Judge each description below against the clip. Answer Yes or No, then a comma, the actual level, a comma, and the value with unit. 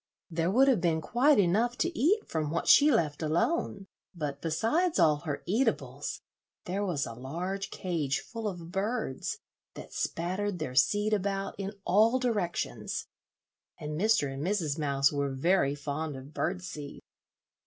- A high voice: No, medium, 175 Hz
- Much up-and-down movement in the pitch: Yes, wide, 5.9 semitones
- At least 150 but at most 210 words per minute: Yes, average, 155 wpm